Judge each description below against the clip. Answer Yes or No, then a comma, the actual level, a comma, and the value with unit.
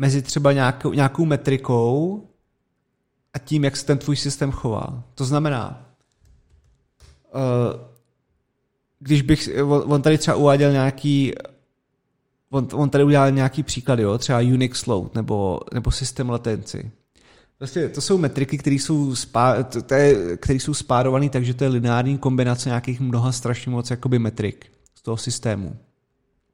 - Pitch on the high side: No, low, 130 Hz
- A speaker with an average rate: Yes, average, 135 wpm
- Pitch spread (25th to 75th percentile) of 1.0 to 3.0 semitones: Yes, average, 2.7 semitones